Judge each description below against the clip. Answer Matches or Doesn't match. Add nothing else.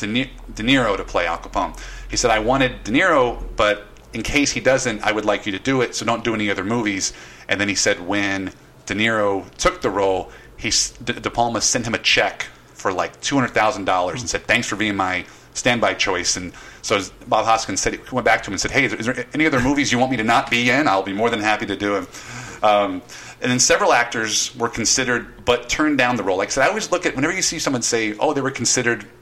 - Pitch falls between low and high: Doesn't match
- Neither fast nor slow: Doesn't match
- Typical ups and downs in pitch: Matches